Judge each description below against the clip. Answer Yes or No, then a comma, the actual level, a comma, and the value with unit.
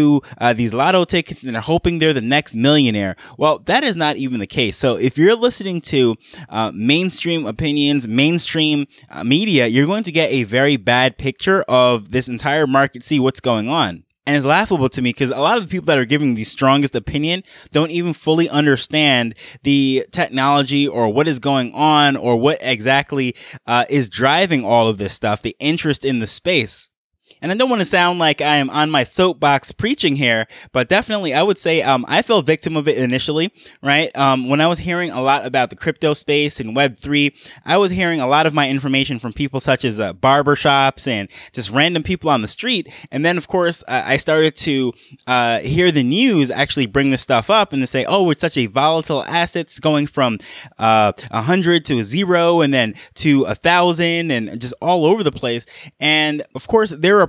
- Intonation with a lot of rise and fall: No, average, 4.3 semitones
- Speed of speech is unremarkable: No, fast, 210 wpm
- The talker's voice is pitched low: No, medium, 145 Hz